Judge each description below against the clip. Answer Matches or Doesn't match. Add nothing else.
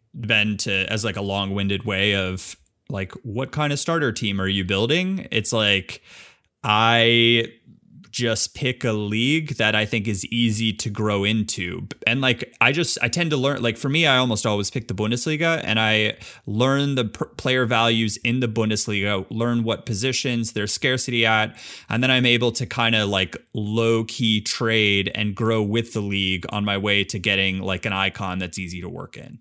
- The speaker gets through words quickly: Doesn't match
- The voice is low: Matches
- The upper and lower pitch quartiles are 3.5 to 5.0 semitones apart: Doesn't match